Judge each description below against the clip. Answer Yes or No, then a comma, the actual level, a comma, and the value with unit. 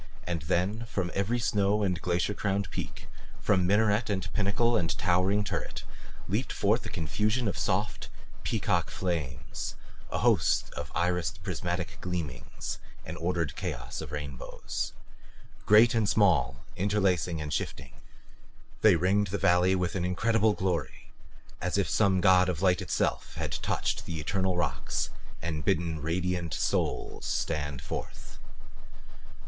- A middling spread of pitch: Yes, average, 3.3 semitones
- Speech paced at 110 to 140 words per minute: Yes, slow, 135 wpm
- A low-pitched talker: Yes, very low, 90 Hz